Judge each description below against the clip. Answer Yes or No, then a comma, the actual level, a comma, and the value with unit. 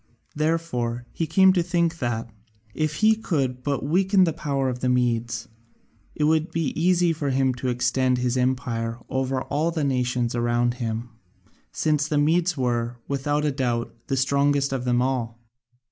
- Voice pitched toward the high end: No, low, 135 Hz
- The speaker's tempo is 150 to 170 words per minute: Yes, average, 160 wpm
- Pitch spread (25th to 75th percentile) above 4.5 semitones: No, average, 4.1 semitones